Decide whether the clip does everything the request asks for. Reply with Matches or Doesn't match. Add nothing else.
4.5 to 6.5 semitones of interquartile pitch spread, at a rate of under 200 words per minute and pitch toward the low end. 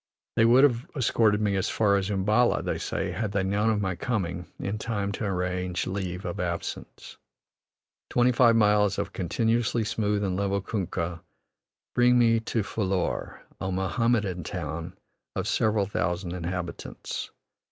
Doesn't match